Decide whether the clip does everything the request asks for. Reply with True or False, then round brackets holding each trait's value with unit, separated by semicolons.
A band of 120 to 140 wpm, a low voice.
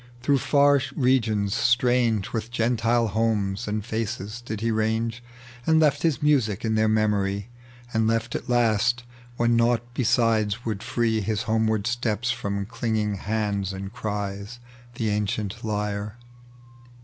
True (135 wpm; 110 Hz)